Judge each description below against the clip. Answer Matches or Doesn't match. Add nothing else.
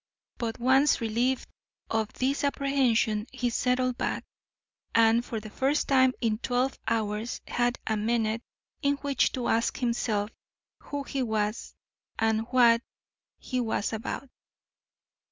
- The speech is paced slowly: Matches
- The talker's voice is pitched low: Doesn't match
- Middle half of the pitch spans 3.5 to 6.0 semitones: Doesn't match